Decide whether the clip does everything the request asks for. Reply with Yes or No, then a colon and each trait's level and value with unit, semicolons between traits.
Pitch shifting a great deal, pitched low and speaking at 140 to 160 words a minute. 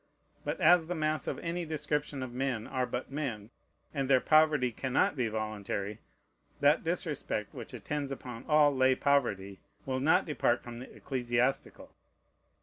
No: average, 3.8 semitones; low, 130 Hz; average, 150 wpm